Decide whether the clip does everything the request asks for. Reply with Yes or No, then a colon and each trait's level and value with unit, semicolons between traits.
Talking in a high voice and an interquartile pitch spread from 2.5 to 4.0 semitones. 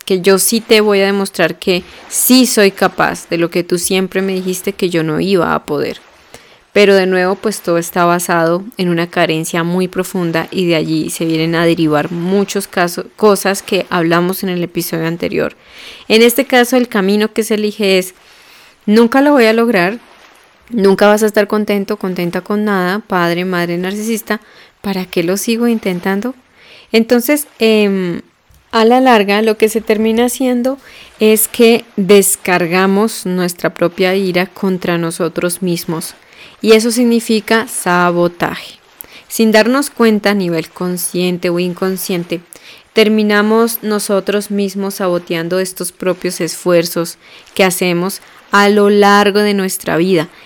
Yes: high, 195 Hz; average, 3.5 semitones